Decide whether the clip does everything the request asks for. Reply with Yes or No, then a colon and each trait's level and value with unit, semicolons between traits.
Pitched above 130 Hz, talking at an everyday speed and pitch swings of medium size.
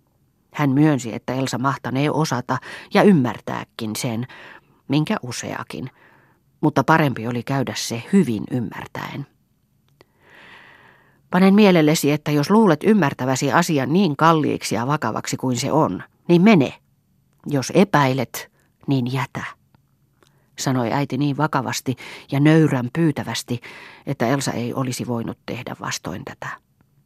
Yes: medium, 140 Hz; average, 120 wpm; average, 3.6 semitones